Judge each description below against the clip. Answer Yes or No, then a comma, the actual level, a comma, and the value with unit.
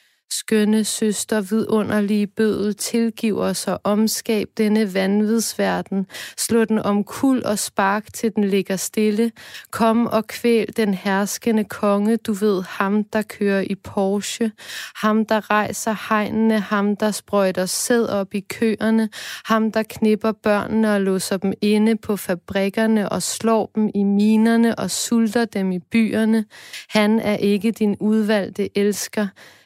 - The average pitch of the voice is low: No, high, 215 Hz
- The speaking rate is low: Yes, slow, 140 wpm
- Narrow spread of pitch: Yes, narrow, 1.6 semitones